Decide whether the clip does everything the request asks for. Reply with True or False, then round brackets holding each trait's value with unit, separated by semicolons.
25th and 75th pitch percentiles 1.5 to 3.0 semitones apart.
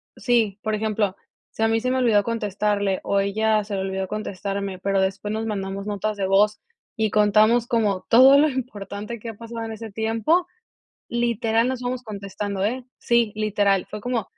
True (2.5 semitones)